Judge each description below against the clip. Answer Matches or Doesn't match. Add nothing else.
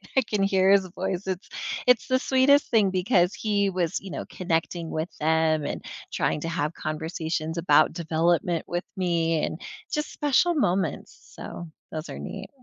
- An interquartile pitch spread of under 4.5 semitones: Matches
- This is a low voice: Doesn't match